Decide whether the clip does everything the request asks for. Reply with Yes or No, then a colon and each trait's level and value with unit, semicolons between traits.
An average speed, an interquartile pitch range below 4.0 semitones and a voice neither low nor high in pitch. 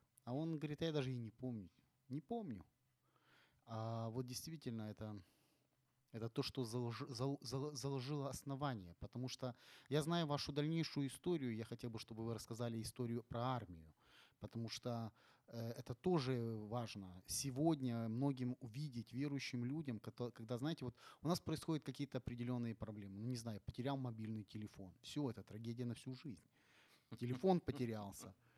No: average, 145 wpm; average, 3.6 semitones; low, 125 Hz